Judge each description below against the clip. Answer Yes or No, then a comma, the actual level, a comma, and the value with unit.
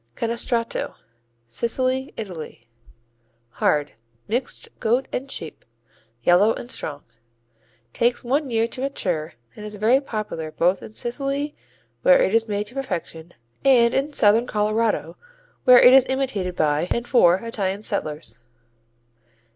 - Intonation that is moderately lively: No, wide, 5.9 semitones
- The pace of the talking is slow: Yes, slow, 130 wpm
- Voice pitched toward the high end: Yes, high, 225 Hz